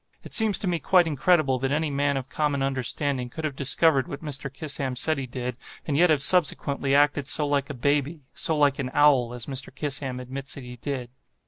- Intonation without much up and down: Yes, narrow, 2.2 semitones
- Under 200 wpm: No, fast, 205 wpm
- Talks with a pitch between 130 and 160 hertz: Yes, medium, 140 Hz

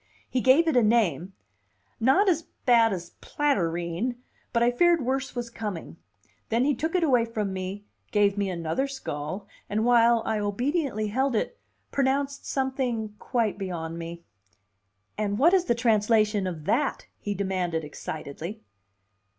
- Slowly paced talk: No, average, 150 wpm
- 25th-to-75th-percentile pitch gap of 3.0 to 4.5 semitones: No, wide, 5.6 semitones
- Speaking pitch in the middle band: No, high, 225 Hz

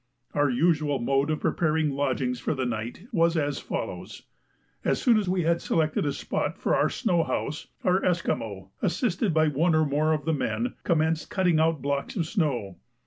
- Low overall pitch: No, medium, 155 Hz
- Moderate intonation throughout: Yes, average, 3.3 semitones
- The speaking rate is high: No, average, 185 wpm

